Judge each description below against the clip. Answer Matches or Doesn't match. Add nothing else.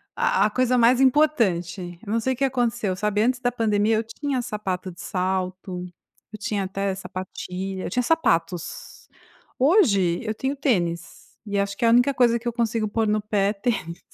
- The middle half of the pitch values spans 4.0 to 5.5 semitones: Matches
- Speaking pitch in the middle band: Doesn't match